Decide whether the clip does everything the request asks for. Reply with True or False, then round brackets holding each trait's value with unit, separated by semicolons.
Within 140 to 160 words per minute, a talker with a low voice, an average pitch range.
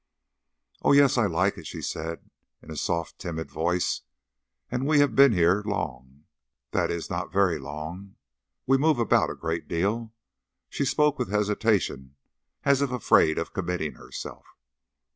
False (155 wpm; 95 Hz; 6.9 semitones)